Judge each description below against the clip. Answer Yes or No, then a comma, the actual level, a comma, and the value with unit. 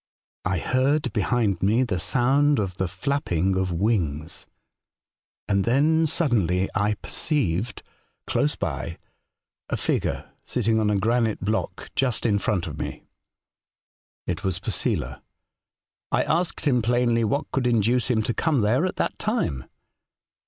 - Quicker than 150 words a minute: No, average, 140 wpm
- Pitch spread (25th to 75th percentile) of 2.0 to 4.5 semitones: No, average, 5.2 semitones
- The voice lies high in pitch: No, low, 110 Hz